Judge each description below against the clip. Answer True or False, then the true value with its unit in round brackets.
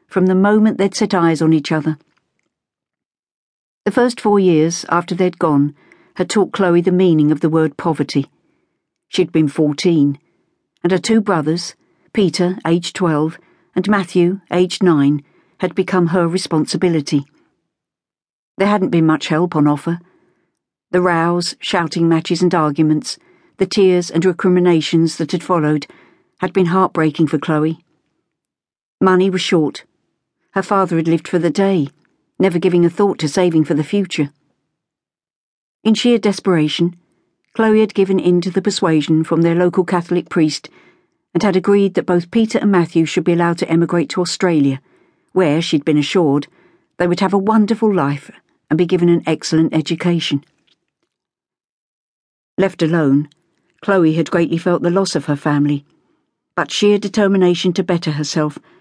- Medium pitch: True (175 Hz)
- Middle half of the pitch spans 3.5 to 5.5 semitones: False (3.0 semitones)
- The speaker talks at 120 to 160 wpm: True (155 wpm)